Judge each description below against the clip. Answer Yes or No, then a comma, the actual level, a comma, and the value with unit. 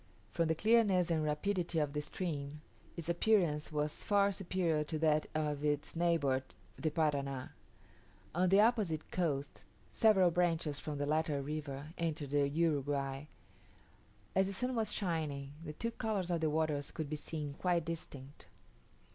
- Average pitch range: Yes, average, 3.3 semitones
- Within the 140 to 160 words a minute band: Yes, average, 155 wpm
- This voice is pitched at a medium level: Yes, medium, 155 Hz